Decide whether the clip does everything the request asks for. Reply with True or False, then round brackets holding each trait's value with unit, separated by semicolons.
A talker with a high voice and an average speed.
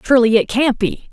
False (240 Hz; 215 wpm)